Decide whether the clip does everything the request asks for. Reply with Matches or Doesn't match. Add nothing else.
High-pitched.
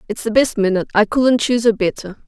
Matches